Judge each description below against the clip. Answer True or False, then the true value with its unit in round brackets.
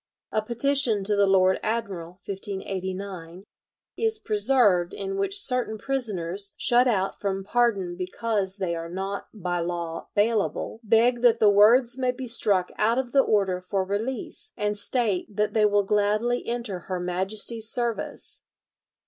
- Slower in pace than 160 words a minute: True (150 wpm)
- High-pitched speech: True (210 Hz)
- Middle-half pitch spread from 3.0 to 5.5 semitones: True (3.9 semitones)